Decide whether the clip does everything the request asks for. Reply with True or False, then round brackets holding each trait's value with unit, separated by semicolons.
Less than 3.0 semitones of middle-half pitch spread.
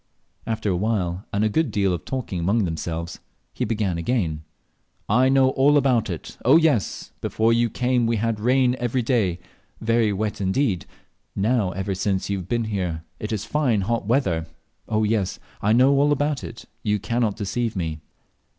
False (4.3 semitones)